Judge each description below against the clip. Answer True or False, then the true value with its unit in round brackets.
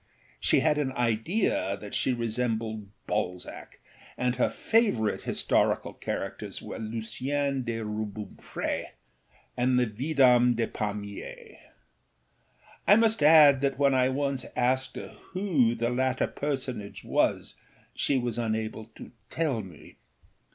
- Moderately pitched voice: False (125 Hz)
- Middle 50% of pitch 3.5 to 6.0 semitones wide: True (4.0 semitones)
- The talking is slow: True (125 wpm)